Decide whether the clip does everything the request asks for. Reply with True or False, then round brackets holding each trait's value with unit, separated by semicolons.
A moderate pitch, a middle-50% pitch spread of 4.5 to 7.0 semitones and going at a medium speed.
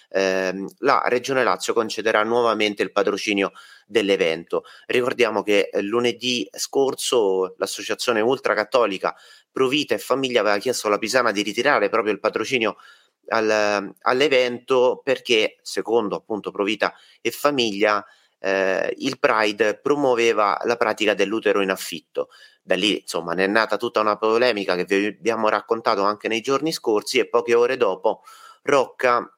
False (115 Hz; 5.2 semitones; 140 wpm)